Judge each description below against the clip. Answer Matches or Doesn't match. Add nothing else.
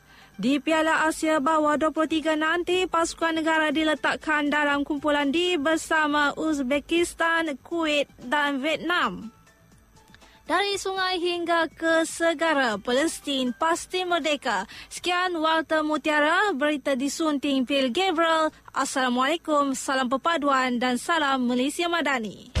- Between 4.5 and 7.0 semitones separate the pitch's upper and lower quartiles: Doesn't match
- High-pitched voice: Matches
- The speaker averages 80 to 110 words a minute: Matches